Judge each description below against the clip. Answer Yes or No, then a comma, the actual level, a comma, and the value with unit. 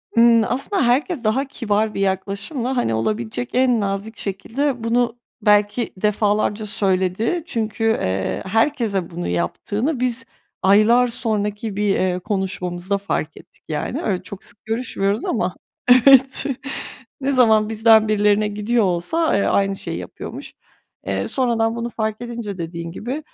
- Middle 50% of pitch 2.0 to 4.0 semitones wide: Yes, average, 3.4 semitones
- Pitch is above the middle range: Yes, high, 215 Hz